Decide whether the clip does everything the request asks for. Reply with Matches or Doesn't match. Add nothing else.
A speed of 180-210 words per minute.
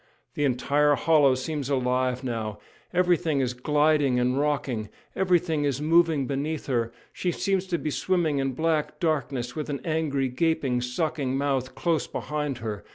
Doesn't match